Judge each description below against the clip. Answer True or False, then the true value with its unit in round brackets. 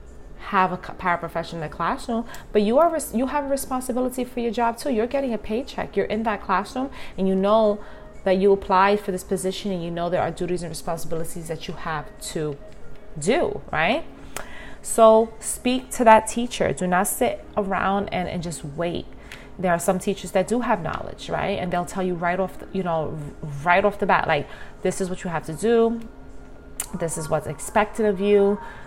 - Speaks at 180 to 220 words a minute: True (200 wpm)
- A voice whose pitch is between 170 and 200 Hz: True (190 Hz)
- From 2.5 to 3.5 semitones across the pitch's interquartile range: False (4.4 semitones)